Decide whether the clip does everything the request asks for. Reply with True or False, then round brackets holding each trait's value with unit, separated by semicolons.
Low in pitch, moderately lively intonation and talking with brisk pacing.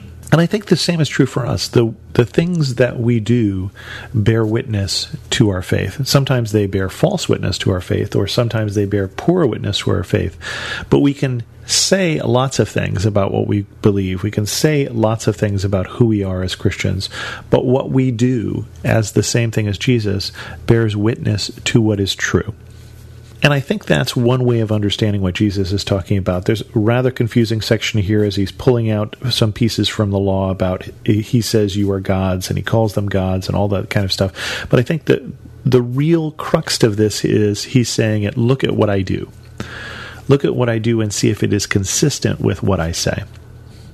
True (110 Hz; 3.2 semitones; 210 wpm)